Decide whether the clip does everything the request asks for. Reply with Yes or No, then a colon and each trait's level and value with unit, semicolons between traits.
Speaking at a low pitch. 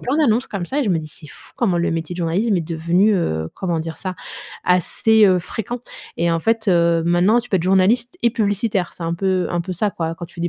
No: medium, 180 Hz